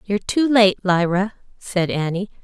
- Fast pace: No, average, 150 wpm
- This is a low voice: No, high, 200 Hz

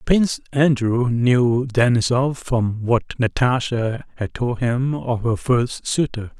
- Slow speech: Yes, slow, 130 wpm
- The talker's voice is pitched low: Yes, low, 125 Hz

